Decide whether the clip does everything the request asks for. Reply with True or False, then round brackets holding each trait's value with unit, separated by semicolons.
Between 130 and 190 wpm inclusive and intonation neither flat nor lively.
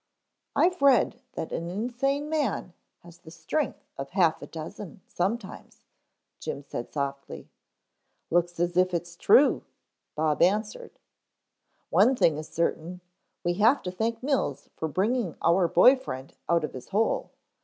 False (145 wpm; 6.4 semitones)